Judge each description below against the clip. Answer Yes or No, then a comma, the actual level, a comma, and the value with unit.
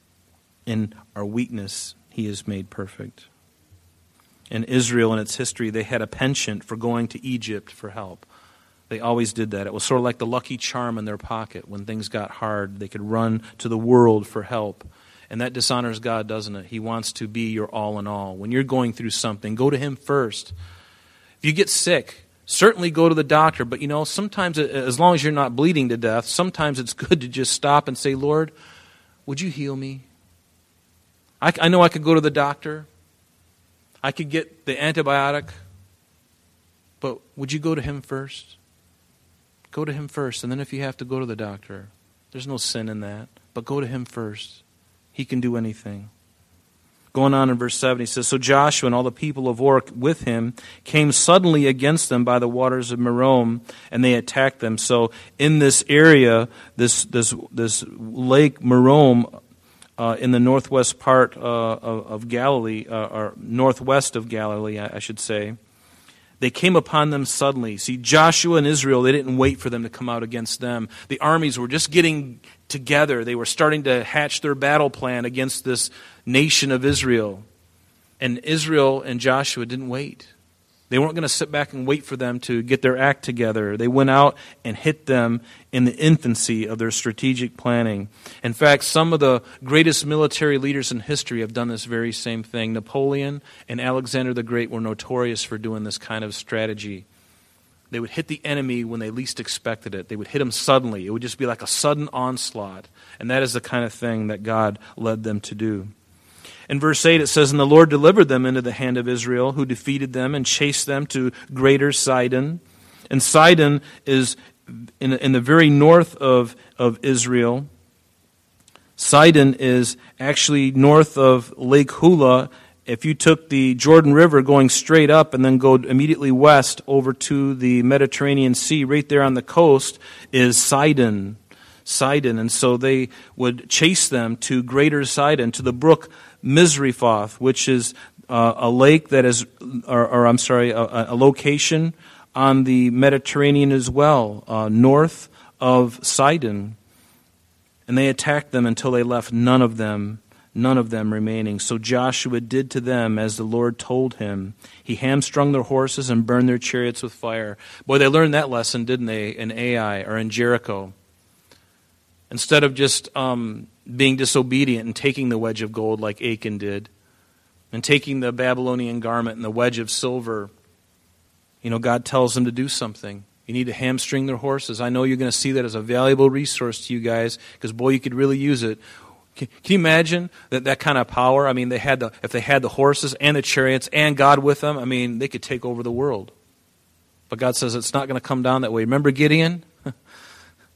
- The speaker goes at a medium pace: Yes, average, 190 wpm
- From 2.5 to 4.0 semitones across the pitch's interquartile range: Yes, average, 3.6 semitones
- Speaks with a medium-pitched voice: No, low, 125 Hz